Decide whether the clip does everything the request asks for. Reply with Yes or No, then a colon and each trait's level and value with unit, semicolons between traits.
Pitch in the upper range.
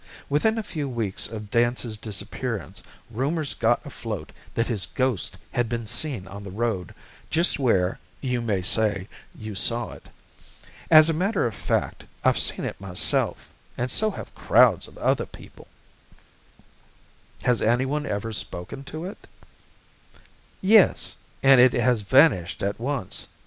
No: low, 120 Hz